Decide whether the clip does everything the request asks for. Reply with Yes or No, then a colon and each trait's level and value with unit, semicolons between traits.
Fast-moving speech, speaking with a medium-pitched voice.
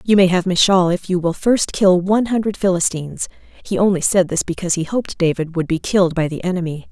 Yes: fast, 225 wpm; medium, 180 Hz